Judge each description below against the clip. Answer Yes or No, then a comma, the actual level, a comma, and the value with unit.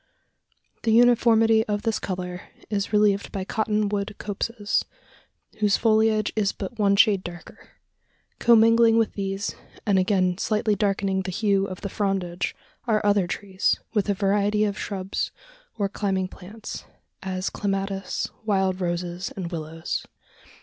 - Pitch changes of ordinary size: No, narrow, 2.1 semitones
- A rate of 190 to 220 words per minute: No, slow, 135 wpm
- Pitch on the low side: No, high, 200 Hz